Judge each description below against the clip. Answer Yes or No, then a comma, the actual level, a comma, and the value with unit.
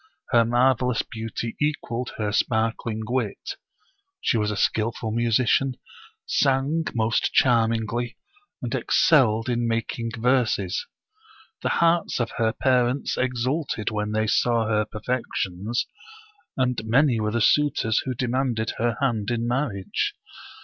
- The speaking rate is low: Yes, slow, 125 wpm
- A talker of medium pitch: No, low, 120 Hz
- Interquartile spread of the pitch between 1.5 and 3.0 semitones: Yes, narrow, 2.5 semitones